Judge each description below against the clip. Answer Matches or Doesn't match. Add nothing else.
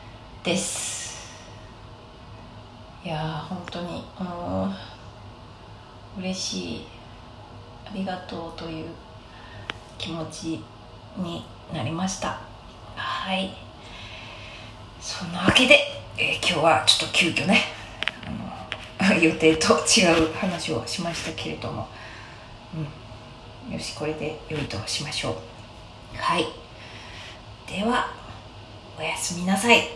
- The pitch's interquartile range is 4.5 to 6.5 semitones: Doesn't match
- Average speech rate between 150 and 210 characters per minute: Matches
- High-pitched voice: Doesn't match